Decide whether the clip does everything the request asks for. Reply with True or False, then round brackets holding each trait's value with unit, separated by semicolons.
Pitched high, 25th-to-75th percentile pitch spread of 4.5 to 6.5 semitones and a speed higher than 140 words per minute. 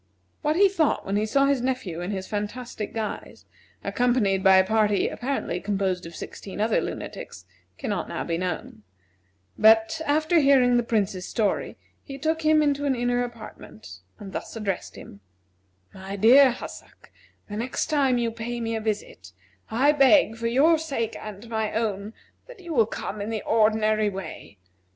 True (225 Hz; 4.8 semitones; 170 wpm)